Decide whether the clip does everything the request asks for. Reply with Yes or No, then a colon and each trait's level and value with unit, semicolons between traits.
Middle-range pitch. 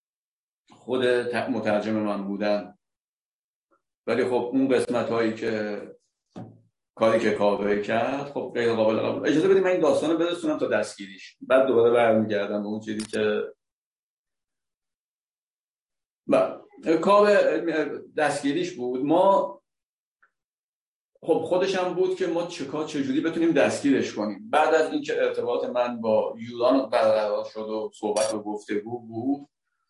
No: low, 120 Hz